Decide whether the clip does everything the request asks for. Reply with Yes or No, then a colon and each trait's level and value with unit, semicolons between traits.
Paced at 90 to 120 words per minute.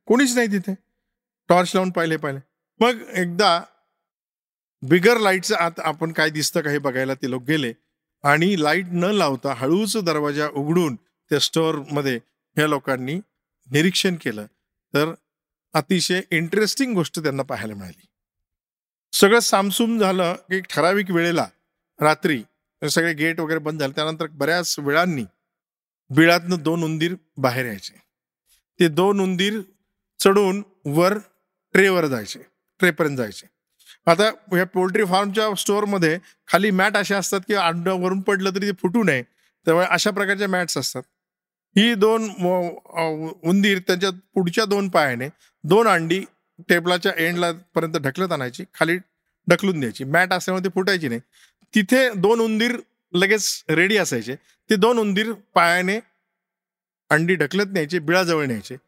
No: fast, 130 wpm